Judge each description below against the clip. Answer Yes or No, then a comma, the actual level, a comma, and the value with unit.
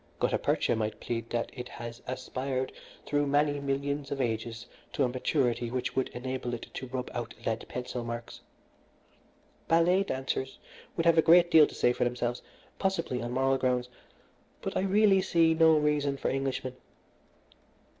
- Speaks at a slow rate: No, average, 165 wpm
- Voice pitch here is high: No, low, 130 Hz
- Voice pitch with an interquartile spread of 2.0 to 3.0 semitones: No, average, 3.4 semitones